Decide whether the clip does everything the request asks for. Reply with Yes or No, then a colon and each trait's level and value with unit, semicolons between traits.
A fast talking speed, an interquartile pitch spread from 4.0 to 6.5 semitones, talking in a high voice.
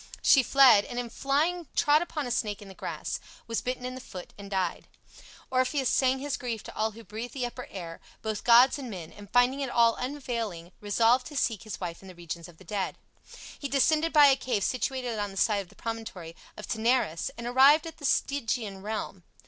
Yes: fast, 215 wpm; average, 4.7 semitones; high, 235 Hz